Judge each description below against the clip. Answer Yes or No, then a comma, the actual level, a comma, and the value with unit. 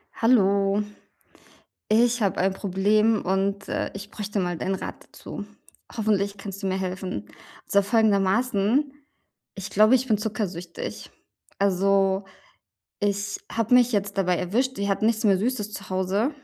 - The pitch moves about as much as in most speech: No, narrow, 2.1 semitones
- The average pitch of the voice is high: Yes, high, 200 Hz